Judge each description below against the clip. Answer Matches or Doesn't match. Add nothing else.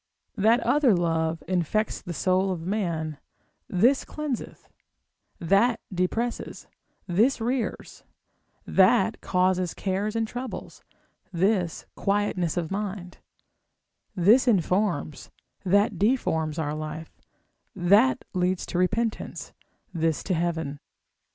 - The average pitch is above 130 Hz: Matches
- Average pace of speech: Doesn't match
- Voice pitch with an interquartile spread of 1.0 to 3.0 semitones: Doesn't match